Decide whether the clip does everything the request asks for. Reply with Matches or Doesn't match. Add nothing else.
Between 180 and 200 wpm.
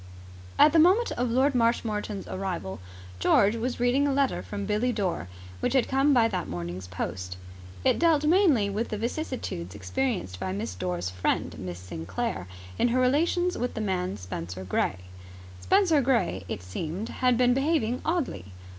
Doesn't match